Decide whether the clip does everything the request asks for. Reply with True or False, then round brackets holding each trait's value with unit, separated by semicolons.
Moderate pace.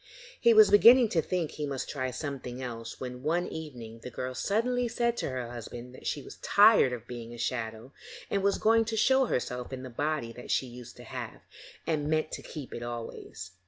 False (210 wpm)